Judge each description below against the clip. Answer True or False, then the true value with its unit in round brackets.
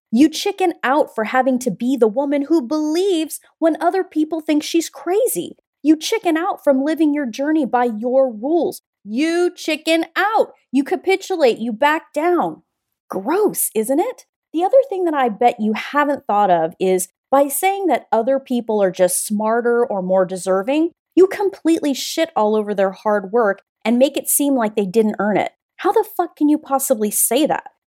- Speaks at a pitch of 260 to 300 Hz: True (285 Hz)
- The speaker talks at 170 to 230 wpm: True (185 wpm)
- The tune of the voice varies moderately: False (6.4 semitones)